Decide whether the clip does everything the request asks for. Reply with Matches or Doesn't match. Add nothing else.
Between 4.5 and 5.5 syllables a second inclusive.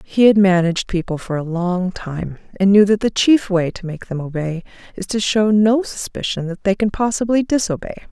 Matches